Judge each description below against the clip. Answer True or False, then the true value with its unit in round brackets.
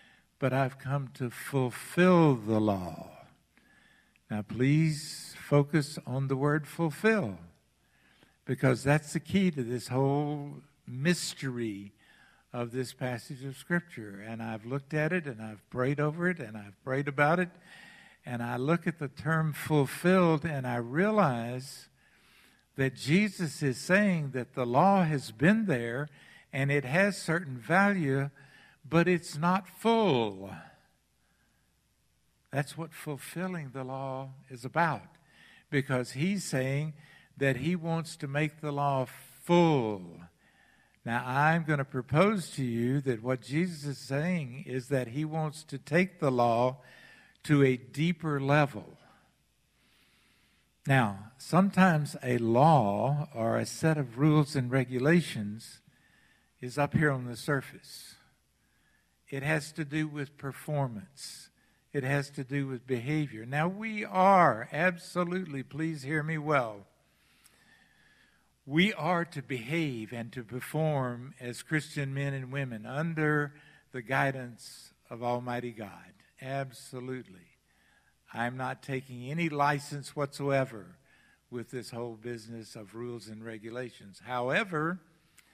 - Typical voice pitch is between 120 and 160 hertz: True (140 Hz)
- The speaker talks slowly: True (130 wpm)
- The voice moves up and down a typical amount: True (4.0 semitones)